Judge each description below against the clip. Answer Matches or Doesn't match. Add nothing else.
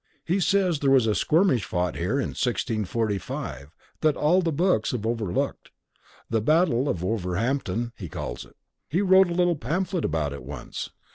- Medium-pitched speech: Doesn't match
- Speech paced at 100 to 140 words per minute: Doesn't match